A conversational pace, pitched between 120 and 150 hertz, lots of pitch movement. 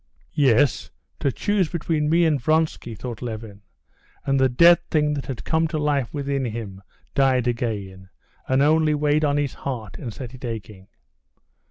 No: average, 170 wpm; low, 135 Hz; average, 4.6 semitones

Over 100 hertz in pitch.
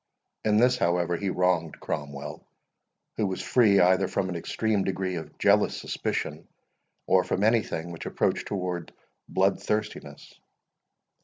No: very low, 95 Hz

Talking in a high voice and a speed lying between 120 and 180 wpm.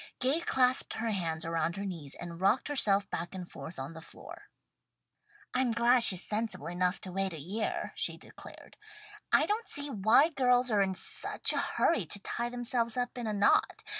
No: high, 210 Hz; average, 190 wpm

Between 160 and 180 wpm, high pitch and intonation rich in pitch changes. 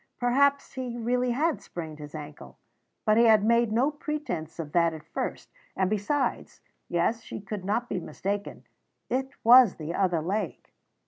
Yes: average, 165 wpm; high, 215 Hz; wide, 6.4 semitones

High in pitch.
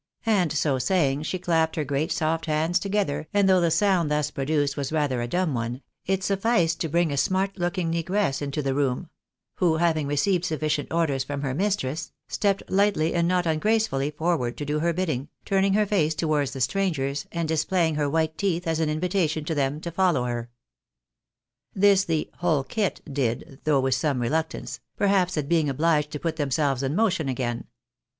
No: medium, 160 Hz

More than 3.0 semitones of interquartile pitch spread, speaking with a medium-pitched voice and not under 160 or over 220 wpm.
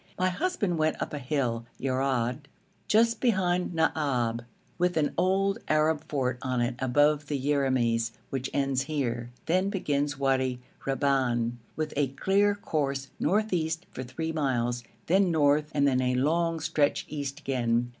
No: average, 4.0 semitones; medium, 145 Hz; average, 150 wpm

